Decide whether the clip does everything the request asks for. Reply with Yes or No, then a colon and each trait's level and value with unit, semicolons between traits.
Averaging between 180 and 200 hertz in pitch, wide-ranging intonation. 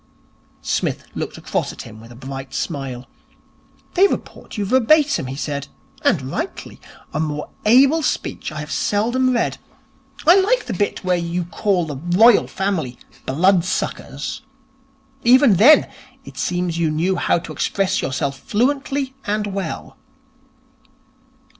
Yes: medium, 185 Hz; wide, 8.2 semitones